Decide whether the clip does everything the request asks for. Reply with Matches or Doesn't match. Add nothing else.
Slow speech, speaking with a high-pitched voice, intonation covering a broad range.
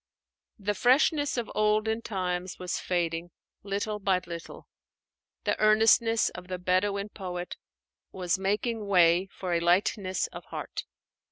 Doesn't match